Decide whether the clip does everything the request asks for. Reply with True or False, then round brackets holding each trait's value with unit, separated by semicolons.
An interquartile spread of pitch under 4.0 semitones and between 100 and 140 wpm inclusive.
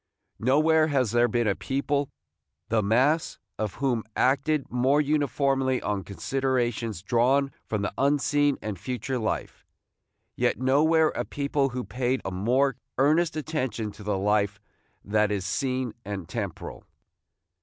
False (4.6 semitones; 135 wpm)